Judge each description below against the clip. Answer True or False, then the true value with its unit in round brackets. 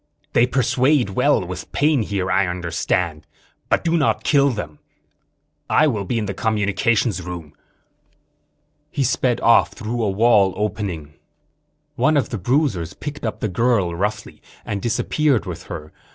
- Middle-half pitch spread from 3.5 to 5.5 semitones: True (5.2 semitones)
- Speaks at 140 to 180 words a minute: True (150 wpm)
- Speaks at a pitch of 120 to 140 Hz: False (110 Hz)